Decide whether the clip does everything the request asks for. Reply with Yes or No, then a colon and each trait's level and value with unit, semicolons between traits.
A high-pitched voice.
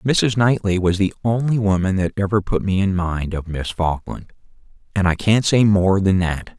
No: low, 100 Hz